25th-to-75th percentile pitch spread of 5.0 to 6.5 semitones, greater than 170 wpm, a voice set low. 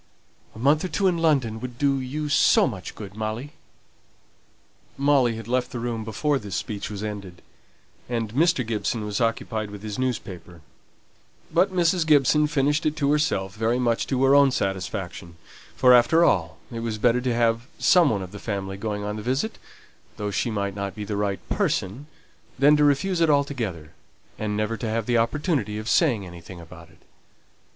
Yes: wide, 5.4 semitones; average, 185 wpm; low, 115 Hz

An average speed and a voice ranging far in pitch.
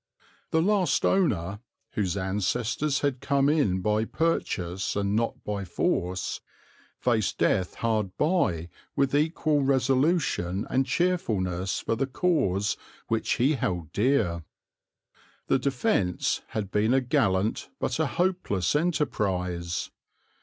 No: slow, 120 wpm; wide, 7.1 semitones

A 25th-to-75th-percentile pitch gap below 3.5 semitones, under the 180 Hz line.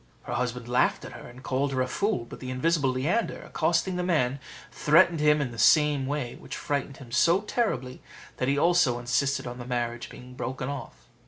No: average, 3.8 semitones; low, 135 Hz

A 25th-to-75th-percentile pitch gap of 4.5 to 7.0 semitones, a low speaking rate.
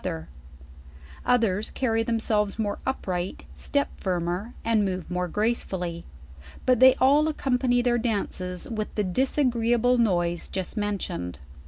Yes: average, 5.0 semitones; slow, 120 wpm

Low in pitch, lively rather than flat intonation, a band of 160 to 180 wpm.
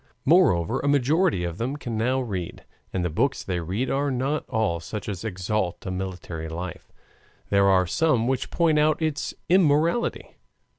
Yes: low, 115 Hz; wide, 7.8 semitones; average, 165 wpm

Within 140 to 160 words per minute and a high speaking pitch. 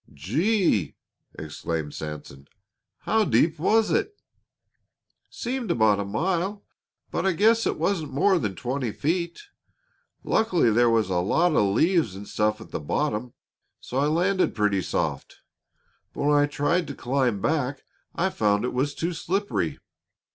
No: average, 145 wpm; medium, 145 Hz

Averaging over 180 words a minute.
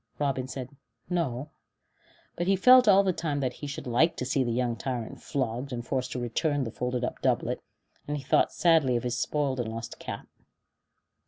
Yes: average, 195 wpm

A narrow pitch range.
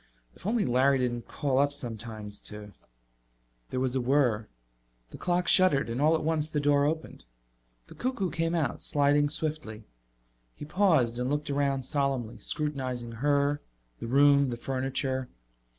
No: average, 3.4 semitones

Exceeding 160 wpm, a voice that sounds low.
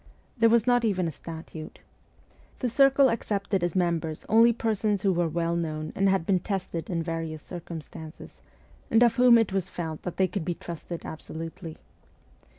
No: average, 170 wpm; medium, 180 Hz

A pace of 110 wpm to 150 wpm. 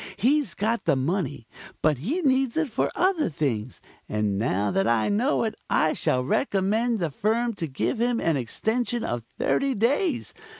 No: average, 170 wpm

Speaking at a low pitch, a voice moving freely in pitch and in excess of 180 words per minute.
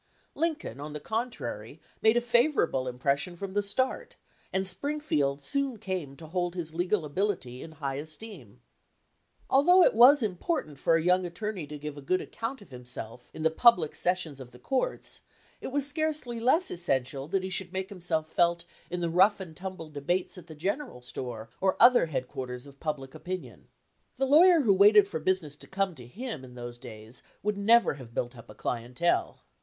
No: medium, 175 Hz; wide, 7.2 semitones; average, 190 wpm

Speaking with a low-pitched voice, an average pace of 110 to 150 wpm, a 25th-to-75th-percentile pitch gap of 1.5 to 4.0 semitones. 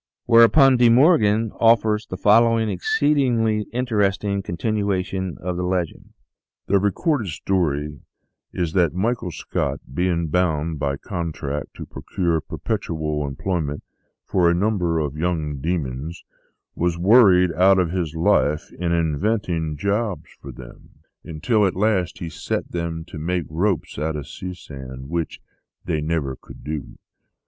No: very low, 90 Hz; average, 140 wpm; average, 4.9 semitones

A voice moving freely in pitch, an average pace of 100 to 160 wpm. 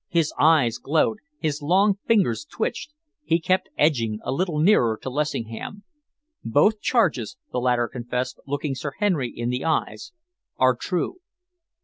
Yes: wide, 7.0 semitones; average, 140 wpm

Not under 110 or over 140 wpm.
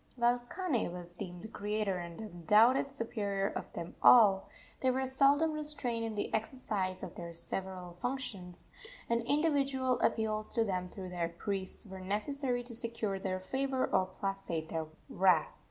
No: average, 155 wpm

